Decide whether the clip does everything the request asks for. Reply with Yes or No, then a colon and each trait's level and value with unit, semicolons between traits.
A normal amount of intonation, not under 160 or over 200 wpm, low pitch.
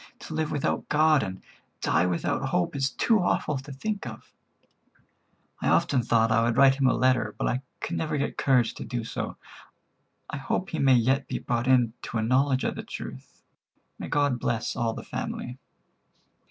Yes: average, 3.4 semitones; average, 185 wpm; low, 130 Hz